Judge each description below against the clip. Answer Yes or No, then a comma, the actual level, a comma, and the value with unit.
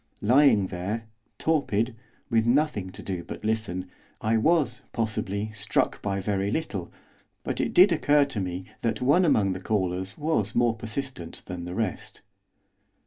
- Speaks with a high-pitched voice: No, low, 110 Hz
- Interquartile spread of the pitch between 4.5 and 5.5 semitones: Yes, average, 5.0 semitones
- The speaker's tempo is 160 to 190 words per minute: No, average, 150 wpm